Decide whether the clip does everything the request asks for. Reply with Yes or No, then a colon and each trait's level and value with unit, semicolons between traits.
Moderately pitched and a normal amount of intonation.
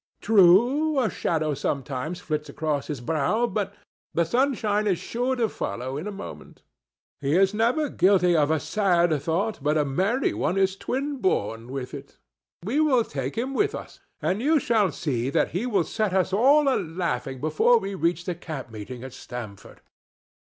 No: medium, 180 Hz; wide, 7.3 semitones